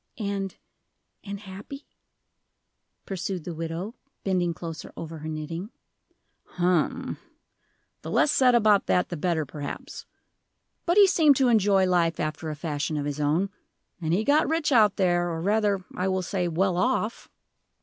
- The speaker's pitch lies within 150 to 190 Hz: Yes, medium, 185 Hz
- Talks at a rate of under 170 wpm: Yes, average, 150 wpm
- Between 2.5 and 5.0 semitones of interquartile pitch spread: Yes, average, 4.2 semitones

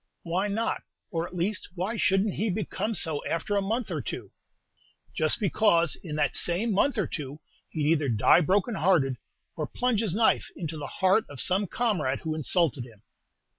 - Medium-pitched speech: Yes, medium, 180 Hz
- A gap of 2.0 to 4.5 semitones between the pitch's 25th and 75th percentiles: No, average, 5.1 semitones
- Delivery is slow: No, average, 185 wpm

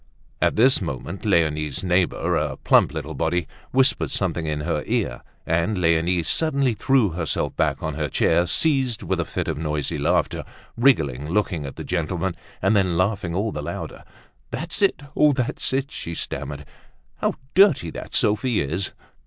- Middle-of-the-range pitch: No, very low, 90 Hz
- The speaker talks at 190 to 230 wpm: No, average, 165 wpm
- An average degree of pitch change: No, wide, 6.2 semitones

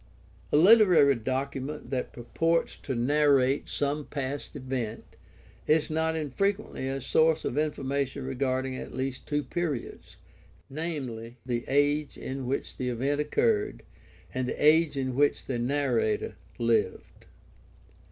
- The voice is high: No, medium, 140 Hz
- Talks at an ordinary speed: No, slow, 125 wpm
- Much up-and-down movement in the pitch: No, average, 3.3 semitones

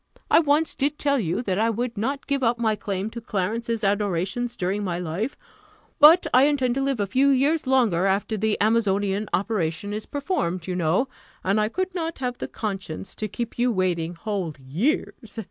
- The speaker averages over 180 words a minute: Yes, average, 190 wpm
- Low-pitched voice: No, high, 220 Hz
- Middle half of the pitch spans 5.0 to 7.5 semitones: Yes, average, 5.3 semitones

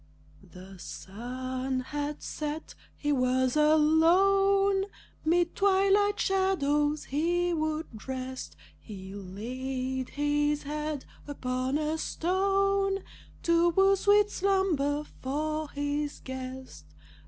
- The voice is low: No, very high, 295 Hz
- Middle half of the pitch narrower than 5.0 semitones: No, average, 5.3 semitones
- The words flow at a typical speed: No, slow, 95 wpm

